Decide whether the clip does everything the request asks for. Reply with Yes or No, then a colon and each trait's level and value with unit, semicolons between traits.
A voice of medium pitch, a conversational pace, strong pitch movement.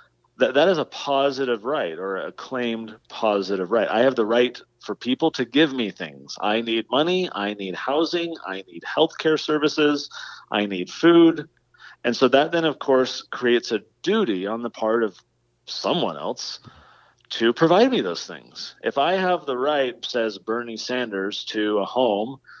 No: low, 120 Hz; average, 175 wpm; wide, 5.9 semitones